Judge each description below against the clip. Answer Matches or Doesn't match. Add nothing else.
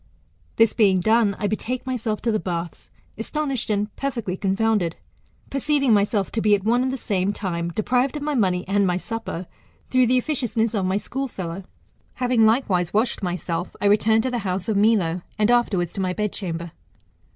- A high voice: Matches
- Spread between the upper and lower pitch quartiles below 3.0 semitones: Doesn't match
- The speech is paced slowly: Doesn't match